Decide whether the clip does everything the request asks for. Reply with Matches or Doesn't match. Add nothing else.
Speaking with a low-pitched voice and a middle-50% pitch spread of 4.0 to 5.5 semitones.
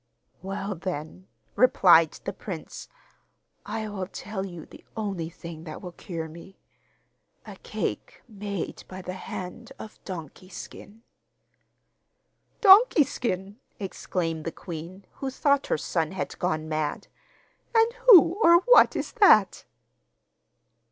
Doesn't match